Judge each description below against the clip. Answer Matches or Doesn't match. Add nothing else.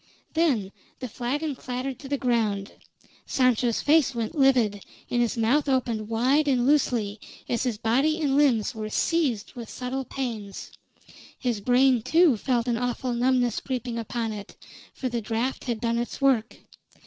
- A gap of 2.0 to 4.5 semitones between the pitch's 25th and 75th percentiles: Matches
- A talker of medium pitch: Doesn't match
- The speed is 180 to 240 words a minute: Doesn't match